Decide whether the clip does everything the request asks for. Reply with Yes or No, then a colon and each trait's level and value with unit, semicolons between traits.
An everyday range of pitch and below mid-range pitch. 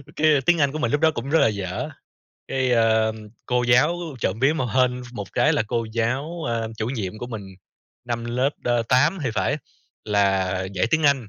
Yes: average, 4.2 semitones; low, 125 Hz